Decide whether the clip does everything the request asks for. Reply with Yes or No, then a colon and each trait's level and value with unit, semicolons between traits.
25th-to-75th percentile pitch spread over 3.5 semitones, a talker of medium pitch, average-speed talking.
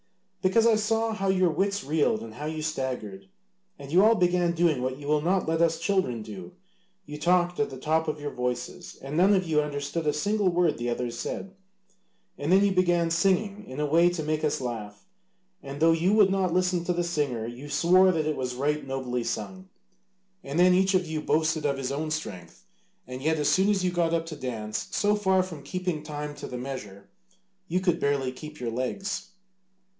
No: average, 5.1 semitones; medium, 155 Hz; fast, 210 wpm